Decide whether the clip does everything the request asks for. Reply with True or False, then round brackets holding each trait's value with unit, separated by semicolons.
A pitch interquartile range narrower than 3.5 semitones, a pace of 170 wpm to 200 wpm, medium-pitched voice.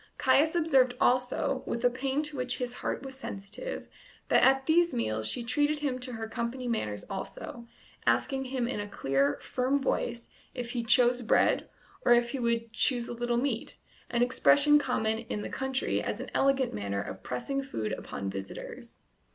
False (2.8 semitones; 180 wpm; 245 Hz)